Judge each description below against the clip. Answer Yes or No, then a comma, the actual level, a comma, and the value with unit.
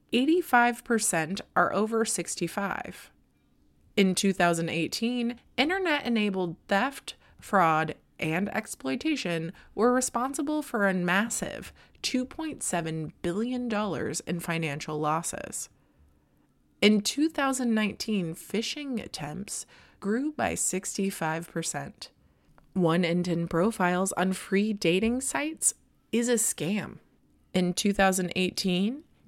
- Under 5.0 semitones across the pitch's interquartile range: No, wide, 5.6 semitones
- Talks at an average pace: No, slow, 85 wpm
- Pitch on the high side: Yes, high, 200 Hz